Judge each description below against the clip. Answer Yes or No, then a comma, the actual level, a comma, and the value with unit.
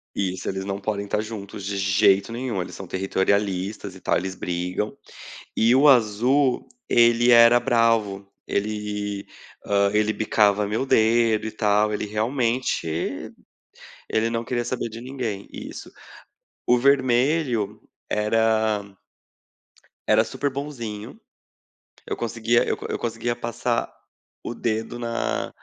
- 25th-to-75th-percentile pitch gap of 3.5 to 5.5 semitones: No, average, 2.8 semitones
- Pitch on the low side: Yes, low, 110 Hz